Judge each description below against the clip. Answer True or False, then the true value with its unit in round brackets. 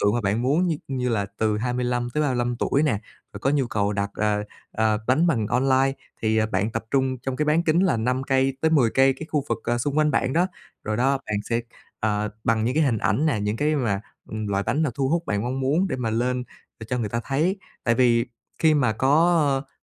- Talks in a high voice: False (125 Hz)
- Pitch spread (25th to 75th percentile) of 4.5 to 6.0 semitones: False (4.1 semitones)